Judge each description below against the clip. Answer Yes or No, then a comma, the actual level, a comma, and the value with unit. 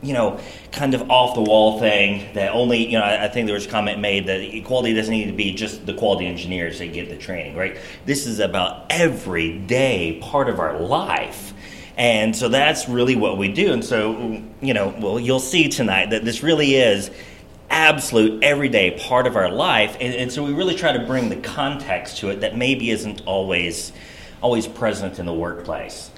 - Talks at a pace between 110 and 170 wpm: No, average, 200 wpm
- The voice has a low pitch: Yes, low, 110 Hz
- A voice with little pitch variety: No, average, 4.1 semitones